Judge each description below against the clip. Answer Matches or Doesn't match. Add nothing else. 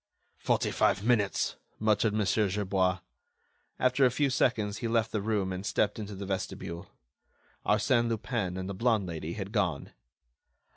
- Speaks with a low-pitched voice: Matches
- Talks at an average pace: Matches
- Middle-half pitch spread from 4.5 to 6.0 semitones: Doesn't match